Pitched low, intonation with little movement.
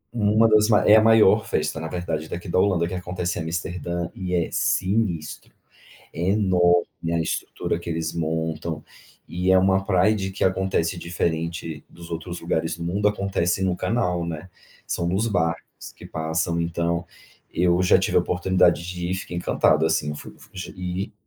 Yes: very low, 90 Hz; narrow, 2.2 semitones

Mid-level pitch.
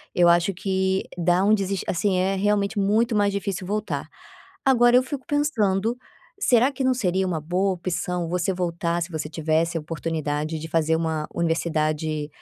Yes: medium, 180 Hz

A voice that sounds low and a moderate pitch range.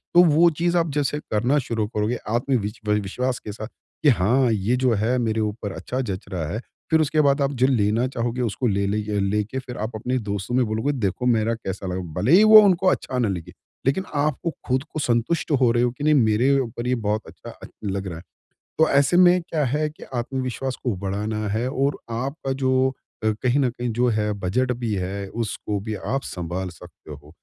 Yes: low, 120 Hz; average, 4.4 semitones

